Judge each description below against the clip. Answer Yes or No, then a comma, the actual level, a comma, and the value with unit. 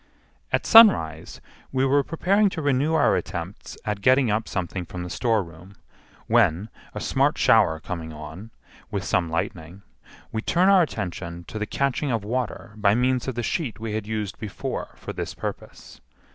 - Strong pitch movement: Yes, wide, 6.4 semitones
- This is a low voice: Yes, low, 110 Hz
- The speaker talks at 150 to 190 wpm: Yes, average, 170 wpm